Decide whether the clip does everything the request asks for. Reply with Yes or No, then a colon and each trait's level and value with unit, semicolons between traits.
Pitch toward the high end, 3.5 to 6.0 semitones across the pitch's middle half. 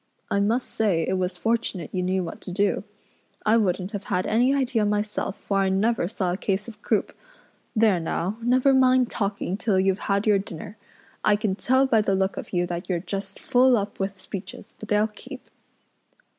No: high, 205 Hz; average, 2.9 semitones